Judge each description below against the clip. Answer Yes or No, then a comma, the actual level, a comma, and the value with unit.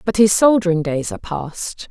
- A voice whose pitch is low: No, medium, 185 Hz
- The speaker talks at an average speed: Yes, average, 190 wpm